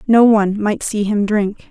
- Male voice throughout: No, female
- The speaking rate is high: Yes, fast, 210 wpm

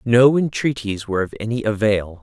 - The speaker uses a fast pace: No, average, 160 wpm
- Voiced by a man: Yes, male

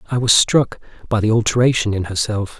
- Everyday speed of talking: Yes, average, 185 wpm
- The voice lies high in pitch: No, low, 110 Hz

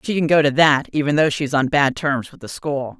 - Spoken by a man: No, female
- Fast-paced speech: Yes, fast, 300 wpm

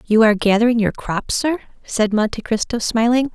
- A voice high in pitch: Yes, high, 230 Hz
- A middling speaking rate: Yes, average, 180 wpm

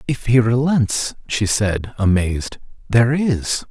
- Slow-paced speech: Yes, slow, 130 wpm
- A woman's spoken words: No, male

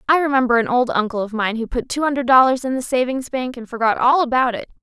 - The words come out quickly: Yes, fast, 260 wpm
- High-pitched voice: Yes, very high, 250 Hz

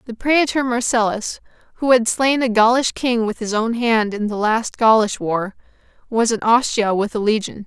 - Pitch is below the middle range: No, high, 230 Hz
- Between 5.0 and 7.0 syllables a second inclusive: No, 4.7 syllables/s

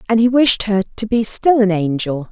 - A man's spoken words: No, female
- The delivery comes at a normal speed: No, fast, 235 wpm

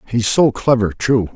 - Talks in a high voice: No, low, 115 Hz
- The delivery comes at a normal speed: Yes, average, 175 wpm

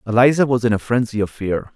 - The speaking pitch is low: Yes, low, 115 Hz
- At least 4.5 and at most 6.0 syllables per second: No, 6.2 syllables/s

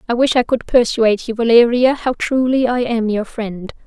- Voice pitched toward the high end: Yes, high, 235 Hz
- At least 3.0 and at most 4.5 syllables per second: No, 5.0 syllables/s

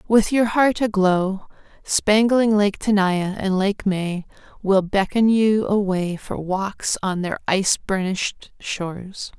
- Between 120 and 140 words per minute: Yes, slow, 135 wpm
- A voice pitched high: Yes, high, 200 Hz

